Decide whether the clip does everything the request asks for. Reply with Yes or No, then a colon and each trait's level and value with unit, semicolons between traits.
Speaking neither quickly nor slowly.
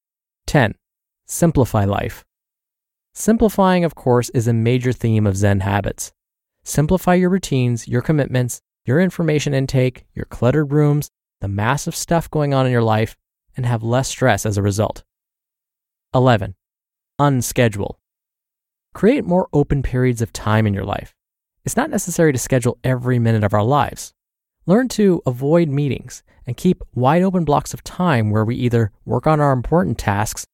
Yes: average, 155 wpm